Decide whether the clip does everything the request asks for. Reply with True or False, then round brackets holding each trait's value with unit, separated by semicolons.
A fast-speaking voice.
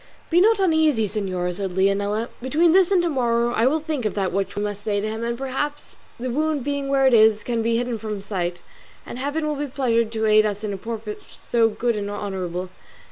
True (235 wpm)